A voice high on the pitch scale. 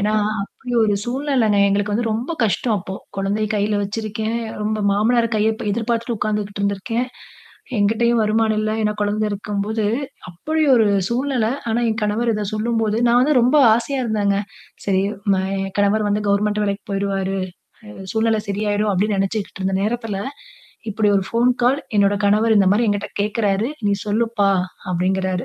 Yes: high, 215 Hz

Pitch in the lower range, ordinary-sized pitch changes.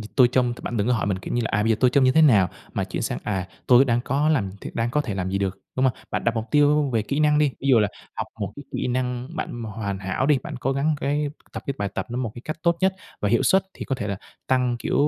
Yes: low, 125 Hz; average, 4.5 semitones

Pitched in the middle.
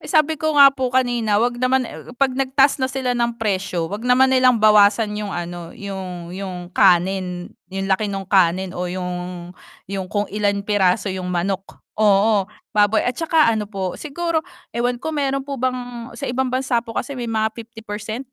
No: high, 215 Hz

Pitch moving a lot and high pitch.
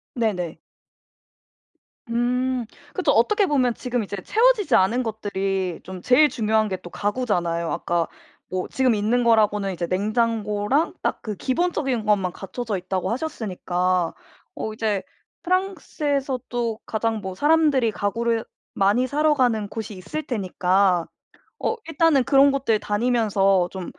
No: average, 4.9 semitones; high, 220 Hz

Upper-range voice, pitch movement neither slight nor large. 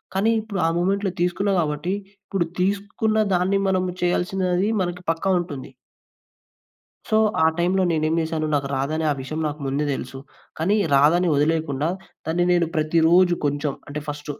No: medium, 170 Hz; average, 3.7 semitones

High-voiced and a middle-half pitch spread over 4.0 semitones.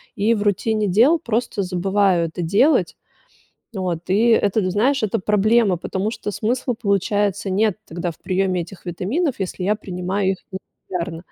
No: high, 200 Hz; average, 3.0 semitones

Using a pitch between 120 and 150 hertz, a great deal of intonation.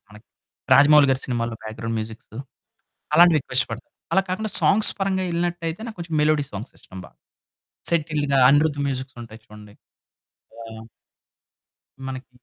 Yes: medium, 140 Hz; wide, 6.3 semitones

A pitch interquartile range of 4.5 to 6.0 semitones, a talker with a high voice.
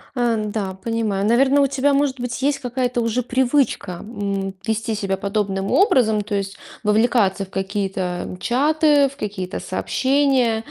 Yes: average, 4.8 semitones; high, 225 Hz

